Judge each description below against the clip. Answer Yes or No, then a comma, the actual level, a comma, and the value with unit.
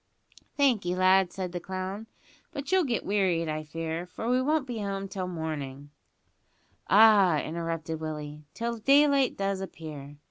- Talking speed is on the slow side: No, average, 150 wpm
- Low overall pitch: No, medium, 185 Hz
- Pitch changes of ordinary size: No, wide, 5.7 semitones